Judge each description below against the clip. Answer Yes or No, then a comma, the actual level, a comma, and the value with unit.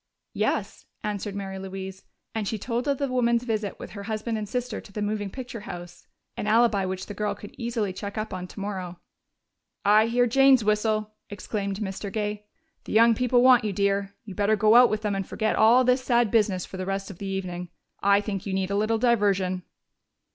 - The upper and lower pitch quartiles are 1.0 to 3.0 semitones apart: Yes, average, 2.7 semitones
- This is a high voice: Yes, high, 210 Hz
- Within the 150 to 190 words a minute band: No, fast, 205 wpm